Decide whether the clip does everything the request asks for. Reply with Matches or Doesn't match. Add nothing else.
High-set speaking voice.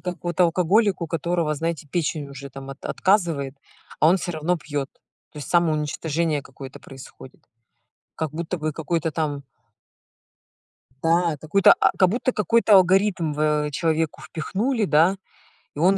Doesn't match